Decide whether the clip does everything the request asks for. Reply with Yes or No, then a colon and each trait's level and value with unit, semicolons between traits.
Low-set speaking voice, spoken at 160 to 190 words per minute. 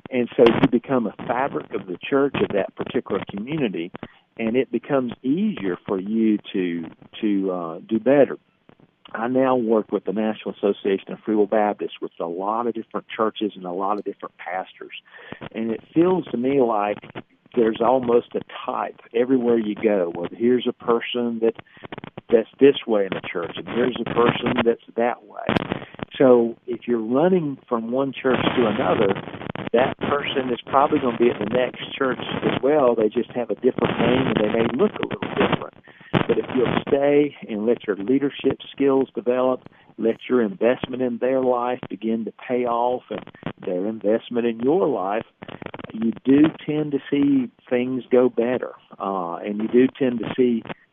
Yes: low, 120 Hz; average, 180 wpm